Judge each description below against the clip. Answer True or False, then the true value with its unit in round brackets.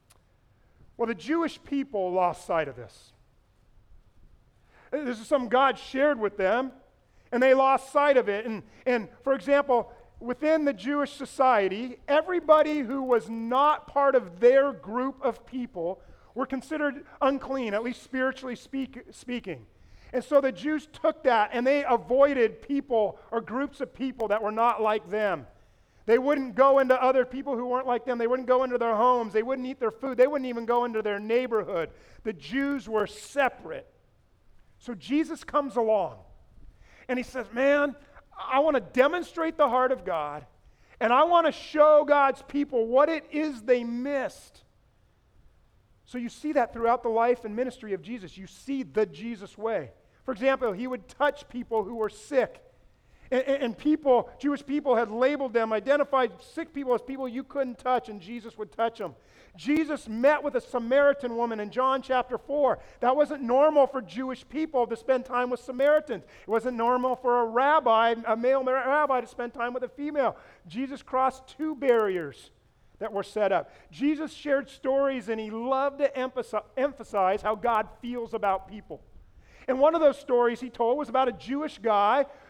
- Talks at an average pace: True (175 wpm)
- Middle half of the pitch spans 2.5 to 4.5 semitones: True (3.4 semitones)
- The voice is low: False (250 Hz)